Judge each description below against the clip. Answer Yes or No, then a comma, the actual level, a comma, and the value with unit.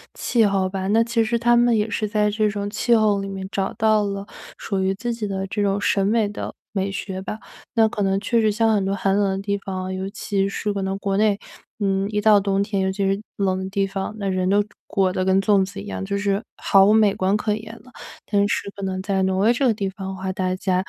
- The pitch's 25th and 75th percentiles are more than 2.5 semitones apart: No, narrow, 1.6 semitones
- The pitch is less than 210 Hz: Yes, high, 200 Hz